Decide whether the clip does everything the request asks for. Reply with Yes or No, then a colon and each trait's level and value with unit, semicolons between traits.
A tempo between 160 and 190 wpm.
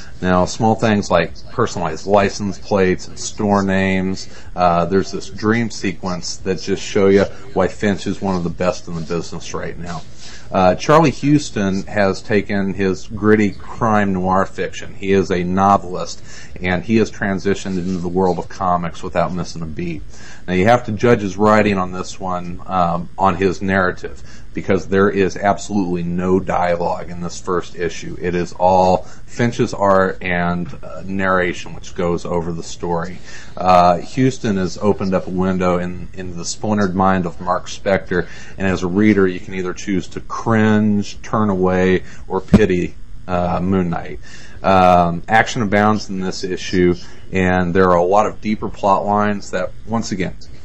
Yes: average, 175 wpm